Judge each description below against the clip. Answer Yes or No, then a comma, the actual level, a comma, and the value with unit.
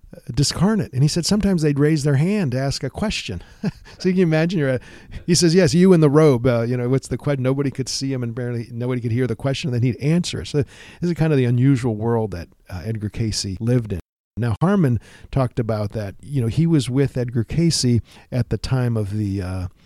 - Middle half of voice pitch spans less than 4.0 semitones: No, average, 5.1 semitones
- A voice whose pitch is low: Yes, low, 130 Hz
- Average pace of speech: No, fast, 240 wpm